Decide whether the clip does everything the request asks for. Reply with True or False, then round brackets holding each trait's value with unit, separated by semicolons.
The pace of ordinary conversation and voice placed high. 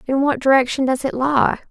False (210 wpm; 265 Hz)